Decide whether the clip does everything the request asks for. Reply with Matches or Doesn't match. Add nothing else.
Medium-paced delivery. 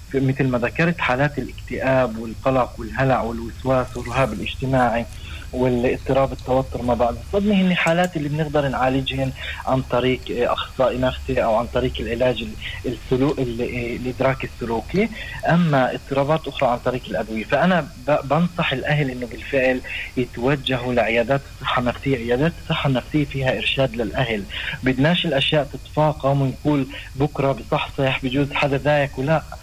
Matches